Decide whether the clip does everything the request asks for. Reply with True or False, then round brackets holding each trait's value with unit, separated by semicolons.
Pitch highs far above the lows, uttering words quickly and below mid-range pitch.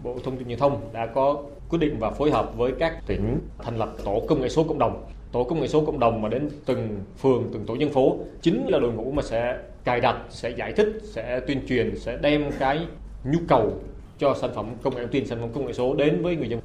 False (4.0 semitones; 260 wpm; 130 Hz)